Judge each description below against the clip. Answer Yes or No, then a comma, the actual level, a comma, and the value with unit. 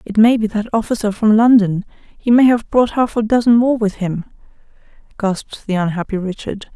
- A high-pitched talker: Yes, high, 215 Hz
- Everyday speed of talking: Yes, average, 185 wpm